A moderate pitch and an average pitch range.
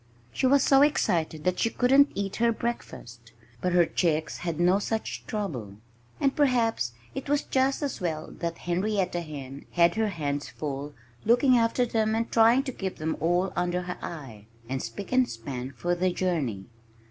No: medium, 180 Hz; wide, 6.9 semitones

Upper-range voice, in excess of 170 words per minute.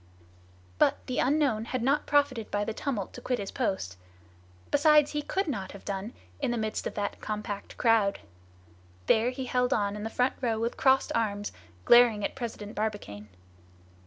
Yes: high, 225 Hz; average, 180 wpm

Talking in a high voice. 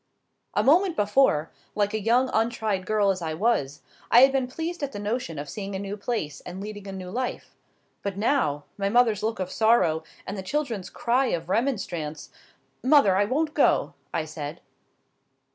Yes: high, 205 Hz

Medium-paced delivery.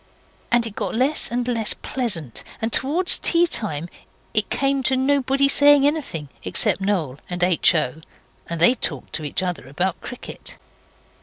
Yes: average, 155 wpm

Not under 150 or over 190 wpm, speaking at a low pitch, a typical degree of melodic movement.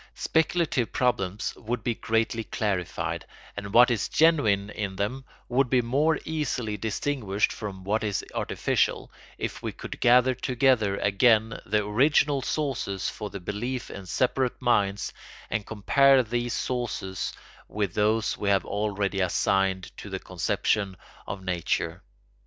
No: slow, 135 wpm; low, 110 Hz; average, 4.1 semitones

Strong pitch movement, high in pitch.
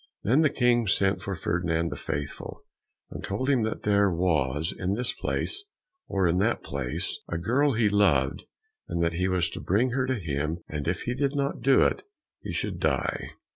No: wide, 6.5 semitones; very low, 95 Hz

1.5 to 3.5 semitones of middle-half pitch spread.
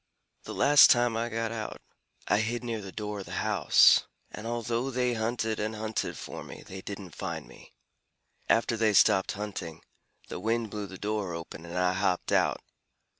Yes: average, 2.9 semitones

